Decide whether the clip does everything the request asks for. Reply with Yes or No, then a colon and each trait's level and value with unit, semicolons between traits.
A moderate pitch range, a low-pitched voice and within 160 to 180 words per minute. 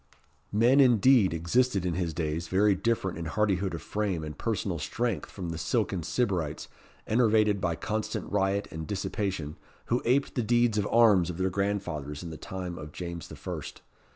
Yes: average, 4.5 semitones; very low, 95 Hz; average, 175 wpm